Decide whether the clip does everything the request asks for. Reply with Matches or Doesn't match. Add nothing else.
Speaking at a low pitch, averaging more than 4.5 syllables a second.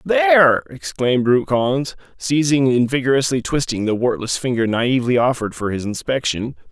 Matches